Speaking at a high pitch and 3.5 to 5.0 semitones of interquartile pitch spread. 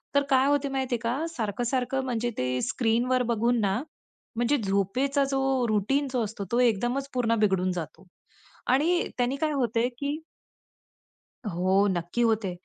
Yes: high, 240 Hz; average, 4.7 semitones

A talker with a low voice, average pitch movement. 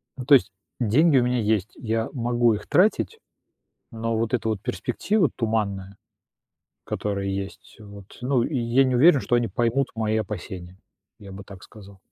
Yes: low, 115 Hz; average, 3.7 semitones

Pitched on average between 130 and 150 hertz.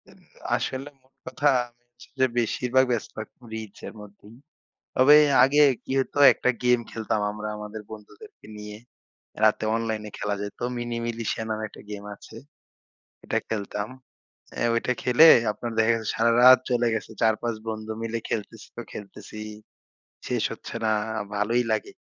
No: low, 115 Hz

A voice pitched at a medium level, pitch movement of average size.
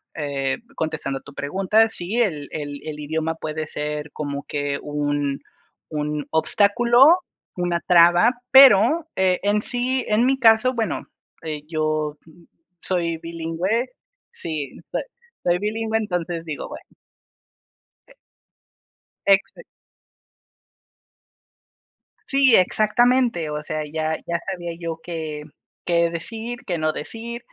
No: medium, 170 Hz; wide, 6.3 semitones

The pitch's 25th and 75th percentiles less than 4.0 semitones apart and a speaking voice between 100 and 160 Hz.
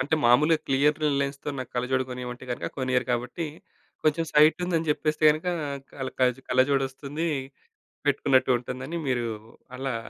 Yes: average, 2.9 semitones; low, 135 Hz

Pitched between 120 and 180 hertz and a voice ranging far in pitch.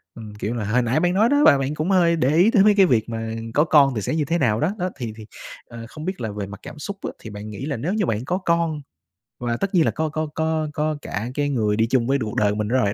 Yes: medium, 140 Hz; wide, 6.6 semitones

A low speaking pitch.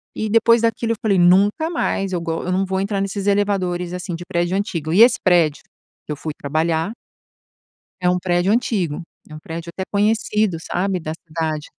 No: medium, 185 Hz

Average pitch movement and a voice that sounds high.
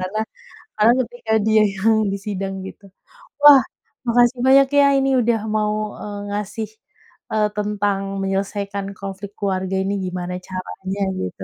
No: narrow, 2.3 semitones; high, 205 Hz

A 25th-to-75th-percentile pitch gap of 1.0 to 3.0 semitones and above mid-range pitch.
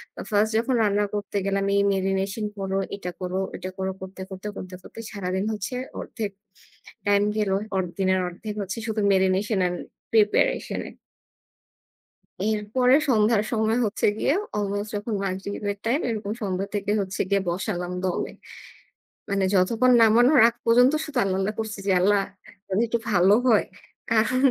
Yes: narrow, 2.4 semitones; high, 205 Hz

